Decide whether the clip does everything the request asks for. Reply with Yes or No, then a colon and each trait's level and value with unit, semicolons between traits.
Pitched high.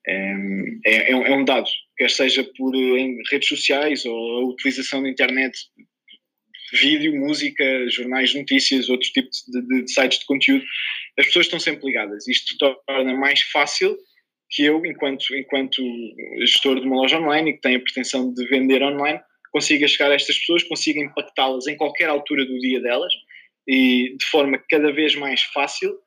No: low, 135 Hz